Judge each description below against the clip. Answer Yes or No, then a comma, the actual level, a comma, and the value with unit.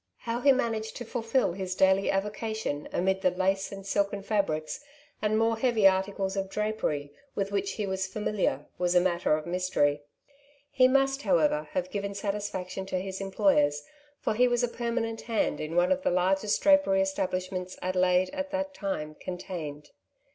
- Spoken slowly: No, average, 170 wpm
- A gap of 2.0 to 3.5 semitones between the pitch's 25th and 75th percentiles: Yes, average, 3.2 semitones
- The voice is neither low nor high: No, high, 195 Hz